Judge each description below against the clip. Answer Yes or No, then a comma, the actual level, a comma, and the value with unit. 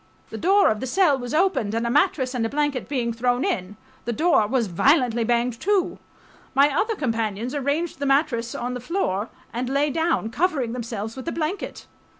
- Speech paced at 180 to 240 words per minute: Yes, average, 190 wpm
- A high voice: Yes, very high, 255 Hz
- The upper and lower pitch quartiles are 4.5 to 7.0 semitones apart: Yes, average, 4.8 semitones